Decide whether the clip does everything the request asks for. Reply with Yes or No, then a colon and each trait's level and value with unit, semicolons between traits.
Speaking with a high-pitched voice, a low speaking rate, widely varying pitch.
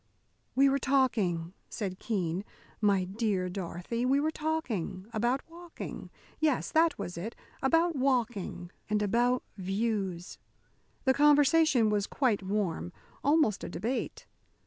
Yes: high, 225 Hz; slow, 125 wpm; wide, 6.2 semitones